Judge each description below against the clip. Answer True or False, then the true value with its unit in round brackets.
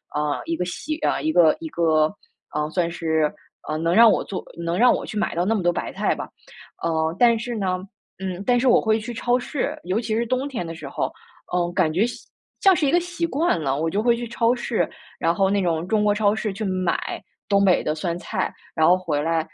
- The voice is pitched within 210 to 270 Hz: False (190 Hz)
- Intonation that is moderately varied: False (5.8 semitones)